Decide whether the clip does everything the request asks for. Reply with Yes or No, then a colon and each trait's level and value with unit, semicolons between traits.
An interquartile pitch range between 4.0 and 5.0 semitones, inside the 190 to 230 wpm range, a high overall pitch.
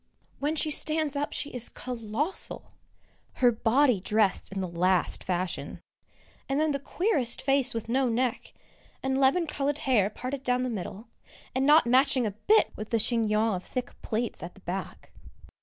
No: average, 4.5 semitones; average, 170 wpm; very high, 250 Hz